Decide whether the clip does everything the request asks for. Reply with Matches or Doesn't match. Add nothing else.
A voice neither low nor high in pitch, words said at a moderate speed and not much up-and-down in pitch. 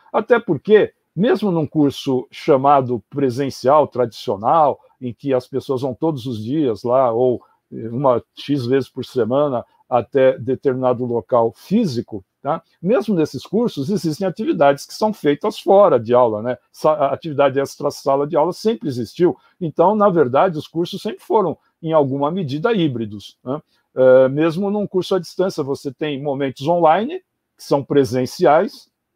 Doesn't match